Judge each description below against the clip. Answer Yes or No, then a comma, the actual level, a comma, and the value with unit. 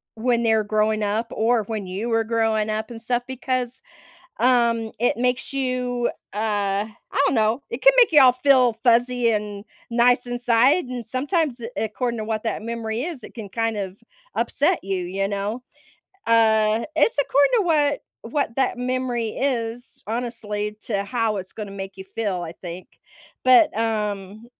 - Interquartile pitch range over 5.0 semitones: No, average, 2.9 semitones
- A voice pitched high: Yes, high, 230 Hz